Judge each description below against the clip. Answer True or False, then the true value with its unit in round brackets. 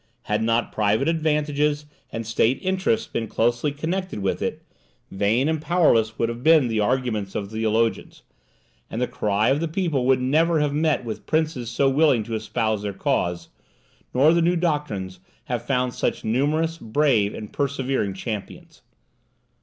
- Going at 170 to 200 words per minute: False (160 wpm)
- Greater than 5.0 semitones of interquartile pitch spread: True (5.6 semitones)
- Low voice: True (125 Hz)